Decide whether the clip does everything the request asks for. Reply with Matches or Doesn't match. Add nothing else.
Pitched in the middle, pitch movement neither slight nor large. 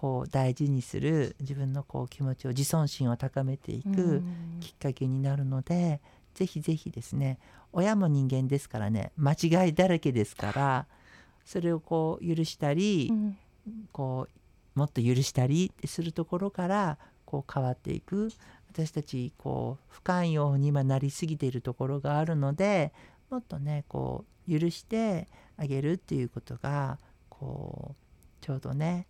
Matches